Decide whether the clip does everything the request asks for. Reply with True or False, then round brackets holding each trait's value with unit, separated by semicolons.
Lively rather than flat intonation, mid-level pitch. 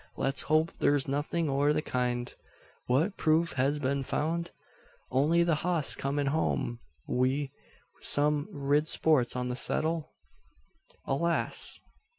False (2.7 semitones; 145 Hz)